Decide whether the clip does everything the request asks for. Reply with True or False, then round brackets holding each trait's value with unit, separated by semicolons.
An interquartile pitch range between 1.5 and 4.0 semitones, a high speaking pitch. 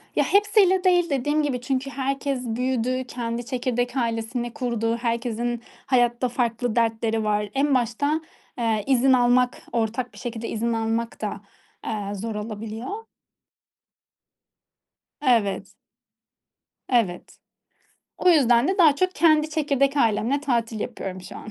True (3.3 semitones; 245 Hz)